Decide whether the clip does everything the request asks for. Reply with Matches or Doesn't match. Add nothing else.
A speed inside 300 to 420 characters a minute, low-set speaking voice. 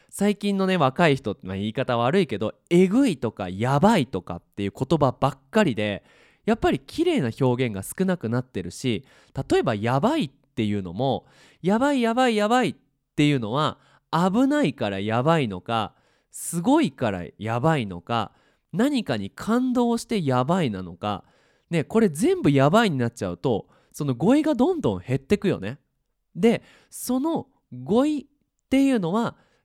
Doesn't match